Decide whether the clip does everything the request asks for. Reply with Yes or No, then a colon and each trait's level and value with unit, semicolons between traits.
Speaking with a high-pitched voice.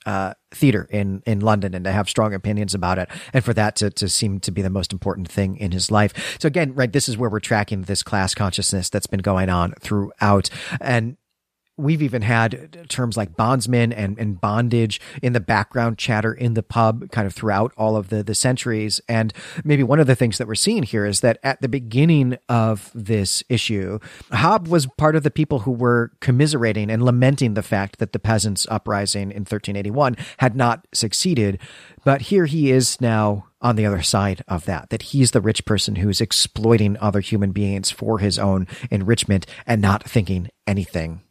No: low, 110 Hz